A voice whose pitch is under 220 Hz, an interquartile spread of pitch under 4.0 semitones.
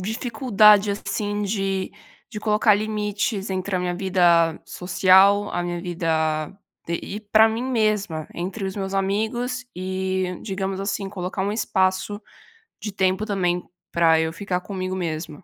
Yes: high, 195 Hz; narrow, 2.6 semitones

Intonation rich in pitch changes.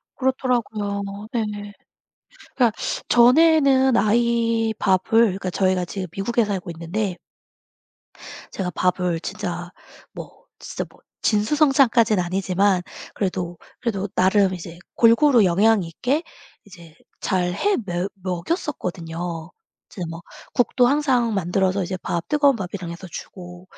No: average, 4.8 semitones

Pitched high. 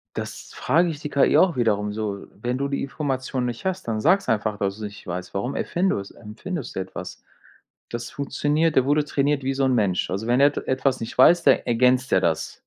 No: low, 130 Hz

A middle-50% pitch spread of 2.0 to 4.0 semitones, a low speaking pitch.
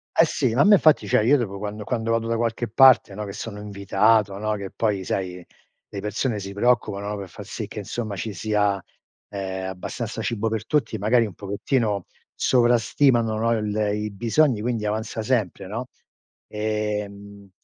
Yes: narrow, 2.4 semitones; low, 105 Hz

